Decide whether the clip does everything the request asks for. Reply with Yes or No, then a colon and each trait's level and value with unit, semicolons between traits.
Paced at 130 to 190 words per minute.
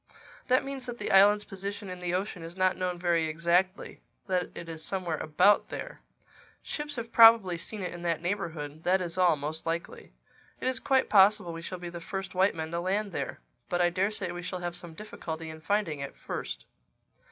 No: average, 200 wpm